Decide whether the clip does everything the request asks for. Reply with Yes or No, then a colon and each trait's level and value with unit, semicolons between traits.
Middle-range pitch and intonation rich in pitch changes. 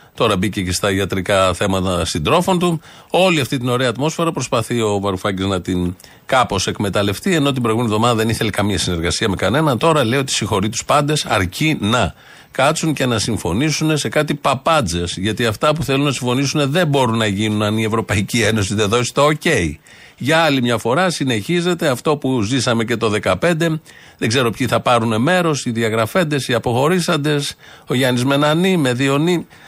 No: low, 125 Hz; wide, 6.2 semitones